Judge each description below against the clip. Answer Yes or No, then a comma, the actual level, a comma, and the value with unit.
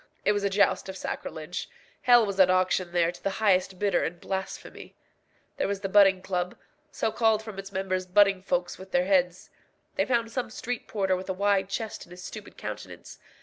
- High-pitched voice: Yes, high, 195 Hz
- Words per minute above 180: Yes, average, 200 wpm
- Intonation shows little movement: Yes, narrow, 1.9 semitones